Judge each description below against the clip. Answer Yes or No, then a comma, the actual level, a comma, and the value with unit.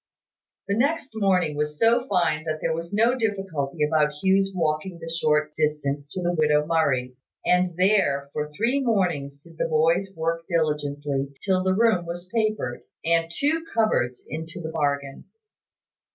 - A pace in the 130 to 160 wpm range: Yes, average, 155 wpm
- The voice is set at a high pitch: No, medium, 165 Hz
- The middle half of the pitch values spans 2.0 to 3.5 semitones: No, average, 4.5 semitones